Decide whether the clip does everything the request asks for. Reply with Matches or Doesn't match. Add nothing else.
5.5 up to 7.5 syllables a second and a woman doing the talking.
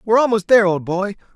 Doesn't match